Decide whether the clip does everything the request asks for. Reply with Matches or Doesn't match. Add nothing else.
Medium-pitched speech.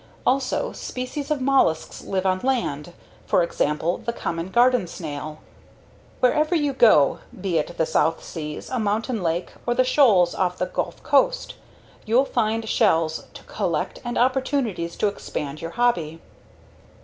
Doesn't match